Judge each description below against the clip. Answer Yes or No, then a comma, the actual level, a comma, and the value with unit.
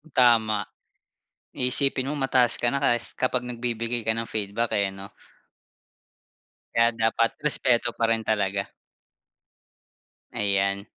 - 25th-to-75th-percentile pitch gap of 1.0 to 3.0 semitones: Yes, average, 2.7 semitones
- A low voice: Yes, low, 115 Hz